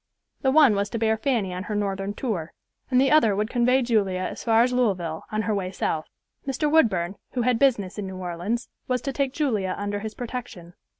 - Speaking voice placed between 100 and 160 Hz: No, high, 220 Hz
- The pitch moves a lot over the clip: No, average, 4.6 semitones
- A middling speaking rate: No, fast, 215 wpm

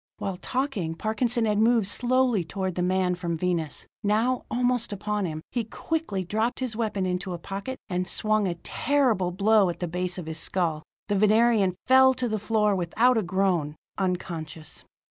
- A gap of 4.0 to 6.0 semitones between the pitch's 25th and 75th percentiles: Yes, average, 4.3 semitones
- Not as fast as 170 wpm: No, average, 175 wpm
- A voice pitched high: Yes, high, 200 Hz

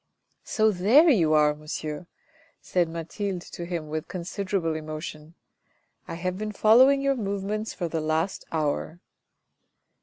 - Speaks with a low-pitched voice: No, medium, 175 Hz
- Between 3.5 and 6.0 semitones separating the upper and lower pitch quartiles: Yes, average, 4.7 semitones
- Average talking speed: Yes, average, 150 wpm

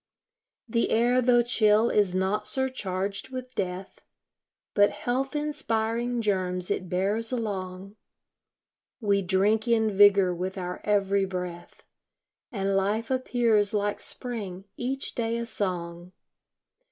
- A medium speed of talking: No, slow, 115 wpm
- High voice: Yes, high, 205 Hz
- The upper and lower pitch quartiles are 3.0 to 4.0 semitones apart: Yes, average, 3.7 semitones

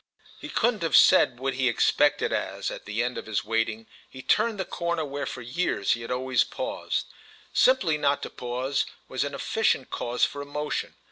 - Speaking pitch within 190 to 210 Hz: No, low, 135 Hz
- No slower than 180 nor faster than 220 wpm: Yes, average, 190 wpm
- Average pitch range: Yes, average, 3.7 semitones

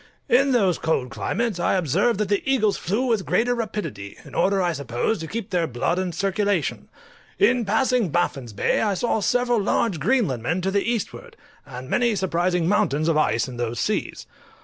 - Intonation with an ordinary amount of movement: No, wide, 6.1 semitones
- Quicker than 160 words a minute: Yes, average, 180 wpm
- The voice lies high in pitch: Yes, high, 195 Hz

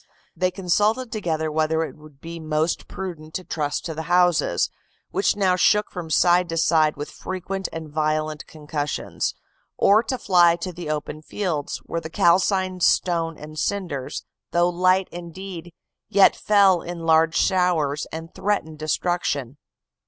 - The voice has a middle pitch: Yes, medium, 170 Hz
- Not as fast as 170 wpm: Yes, average, 150 wpm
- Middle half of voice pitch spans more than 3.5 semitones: No, average, 2.9 semitones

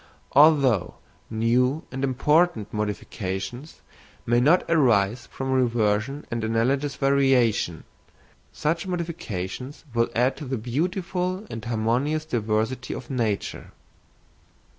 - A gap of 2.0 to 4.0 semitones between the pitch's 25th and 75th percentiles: No, average, 4.7 semitones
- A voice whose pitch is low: Yes, low, 125 Hz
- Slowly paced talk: Yes, slow, 100 wpm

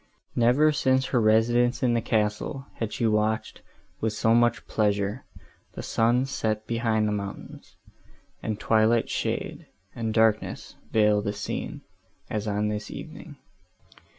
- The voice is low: Yes, low, 110 Hz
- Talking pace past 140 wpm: No, slow, 135 wpm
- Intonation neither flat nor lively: No, narrow, 2.1 semitones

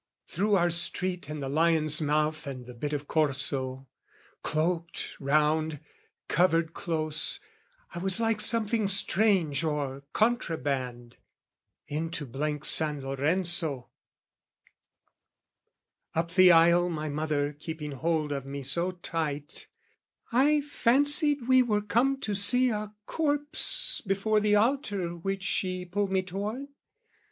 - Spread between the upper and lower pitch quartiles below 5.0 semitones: No, wide, 5.6 semitones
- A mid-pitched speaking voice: Yes, medium, 170 Hz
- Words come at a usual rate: No, slow, 120 wpm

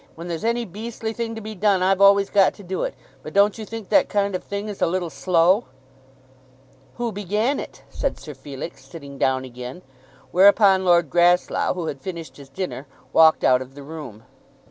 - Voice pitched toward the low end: No, medium, 185 Hz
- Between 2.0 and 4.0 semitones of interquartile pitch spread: No, average, 4.5 semitones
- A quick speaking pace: No, average, 195 wpm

